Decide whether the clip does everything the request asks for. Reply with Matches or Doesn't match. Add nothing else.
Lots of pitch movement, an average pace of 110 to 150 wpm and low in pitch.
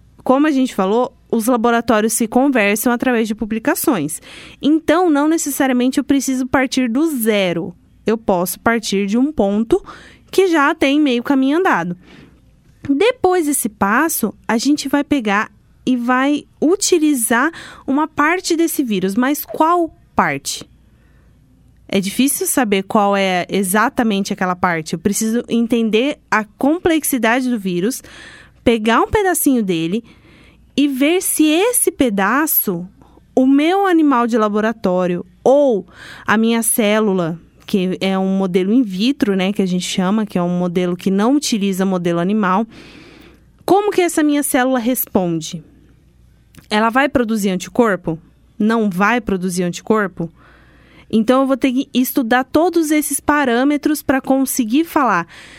Doesn't match